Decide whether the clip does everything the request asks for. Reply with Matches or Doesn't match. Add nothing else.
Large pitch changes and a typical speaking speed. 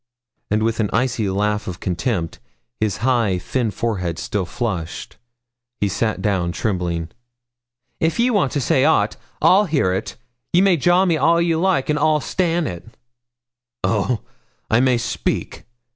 Matches